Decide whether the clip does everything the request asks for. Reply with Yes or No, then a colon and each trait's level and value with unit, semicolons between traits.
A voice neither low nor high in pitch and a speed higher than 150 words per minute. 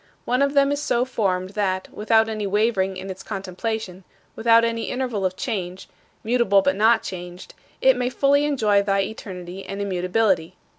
No: high, 205 Hz; average, 165 wpm